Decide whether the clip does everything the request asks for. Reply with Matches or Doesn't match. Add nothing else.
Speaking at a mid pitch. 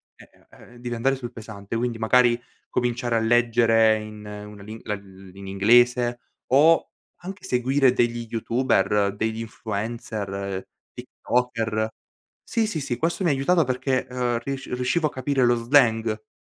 Doesn't match